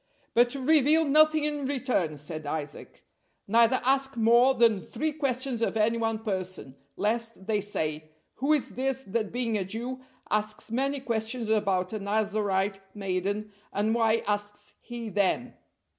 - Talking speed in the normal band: Yes, average, 145 wpm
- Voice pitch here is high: Yes, high, 225 Hz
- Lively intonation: No, average, 4.0 semitones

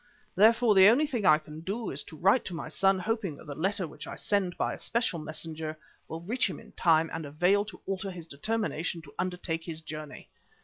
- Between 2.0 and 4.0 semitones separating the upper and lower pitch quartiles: No, average, 4.4 semitones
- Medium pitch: Yes, medium, 180 Hz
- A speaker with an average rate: No, fast, 220 wpm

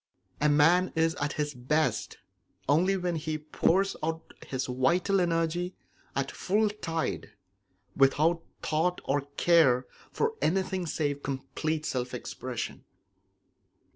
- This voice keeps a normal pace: No, slow, 115 wpm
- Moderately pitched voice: Yes, medium, 160 Hz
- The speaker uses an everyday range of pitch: Yes, average, 3.6 semitones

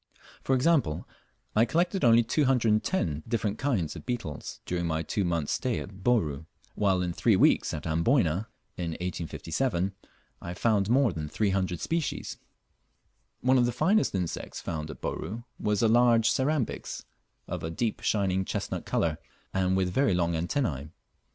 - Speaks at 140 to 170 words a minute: Yes, average, 150 wpm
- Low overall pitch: Yes, low, 100 Hz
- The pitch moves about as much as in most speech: No, wide, 6.4 semitones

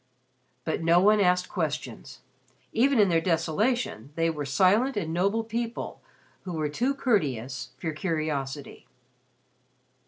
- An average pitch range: No, wide, 5.9 semitones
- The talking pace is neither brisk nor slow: No, slow, 125 wpm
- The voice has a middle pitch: Yes, medium, 170 Hz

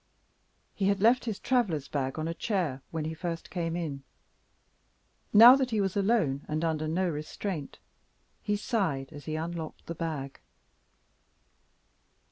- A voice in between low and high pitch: Yes, medium, 165 Hz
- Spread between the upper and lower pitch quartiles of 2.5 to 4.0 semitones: No, average, 4.7 semitones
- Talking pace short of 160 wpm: Yes, average, 145 wpm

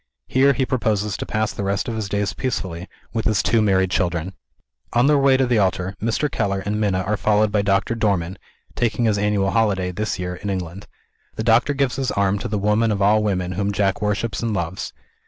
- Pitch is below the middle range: Yes, low, 105 Hz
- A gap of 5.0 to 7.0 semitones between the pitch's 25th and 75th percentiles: No, average, 2.7 semitones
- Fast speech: Yes, fast, 215 wpm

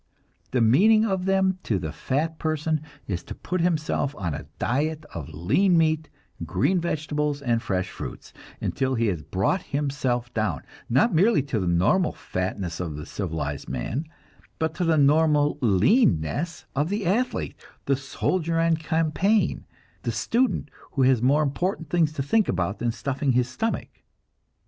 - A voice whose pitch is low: No, medium, 145 Hz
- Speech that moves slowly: No, average, 160 wpm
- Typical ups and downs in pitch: No, wide, 7.1 semitones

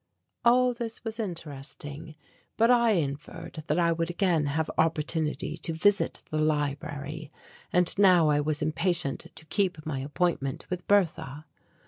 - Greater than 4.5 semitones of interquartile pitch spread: No, average, 3.4 semitones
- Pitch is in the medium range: Yes, medium, 160 Hz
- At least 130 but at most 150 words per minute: Yes, average, 140 wpm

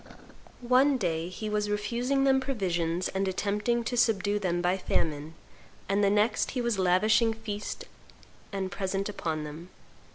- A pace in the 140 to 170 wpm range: Yes, average, 150 wpm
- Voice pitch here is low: No, high, 205 Hz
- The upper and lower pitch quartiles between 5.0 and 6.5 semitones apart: No, average, 3.9 semitones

